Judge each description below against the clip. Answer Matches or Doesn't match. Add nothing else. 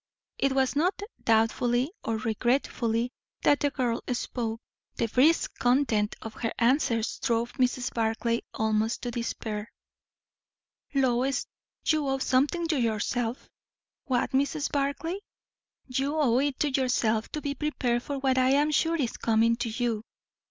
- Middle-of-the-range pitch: Doesn't match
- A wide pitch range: Doesn't match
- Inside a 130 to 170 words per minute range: Matches